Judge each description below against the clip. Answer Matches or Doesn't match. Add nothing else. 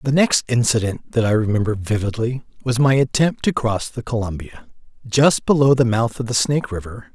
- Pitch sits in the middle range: Doesn't match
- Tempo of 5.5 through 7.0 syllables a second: Doesn't match